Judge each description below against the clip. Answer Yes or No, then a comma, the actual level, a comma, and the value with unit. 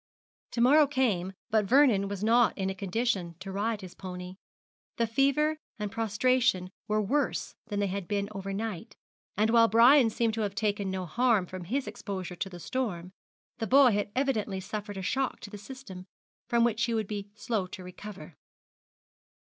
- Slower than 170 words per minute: No, average, 180 wpm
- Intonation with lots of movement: No, average, 3.7 semitones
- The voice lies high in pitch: Yes, high, 210 Hz